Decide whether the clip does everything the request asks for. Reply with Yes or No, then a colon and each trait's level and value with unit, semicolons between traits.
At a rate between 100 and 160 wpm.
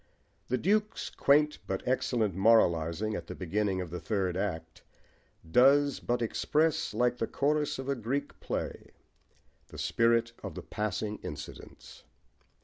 Yes: average, 140 wpm